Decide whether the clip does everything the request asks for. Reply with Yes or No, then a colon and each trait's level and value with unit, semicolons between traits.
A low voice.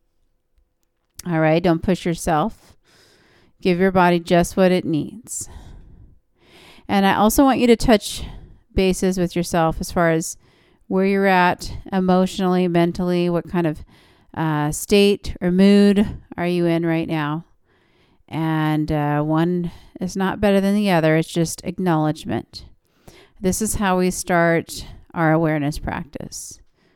No: medium, 175 Hz